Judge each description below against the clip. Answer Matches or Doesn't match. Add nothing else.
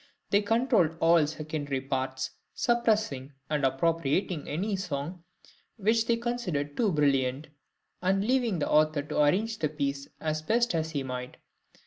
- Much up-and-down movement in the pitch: Matches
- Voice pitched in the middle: Matches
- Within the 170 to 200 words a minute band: Doesn't match